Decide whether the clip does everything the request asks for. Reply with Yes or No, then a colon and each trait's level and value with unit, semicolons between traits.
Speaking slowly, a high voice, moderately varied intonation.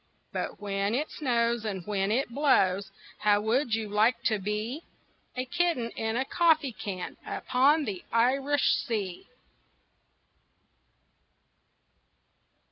Yes: slow, 115 wpm; high, 230 Hz; average, 4.4 semitones